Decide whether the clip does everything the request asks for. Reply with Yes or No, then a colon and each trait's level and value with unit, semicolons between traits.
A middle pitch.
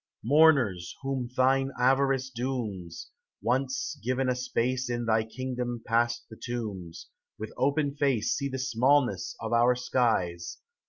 No: low, 125 Hz